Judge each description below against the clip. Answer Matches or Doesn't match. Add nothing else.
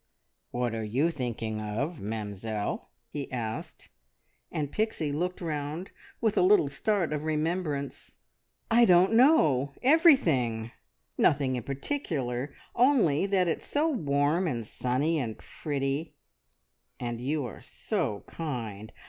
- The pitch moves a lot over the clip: Matches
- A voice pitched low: Doesn't match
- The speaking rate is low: Matches